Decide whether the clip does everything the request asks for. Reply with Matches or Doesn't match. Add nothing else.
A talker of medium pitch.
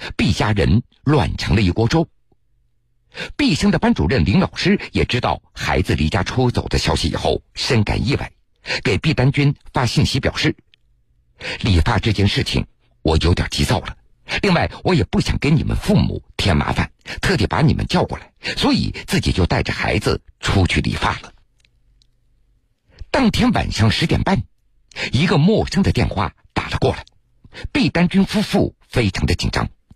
Doesn't match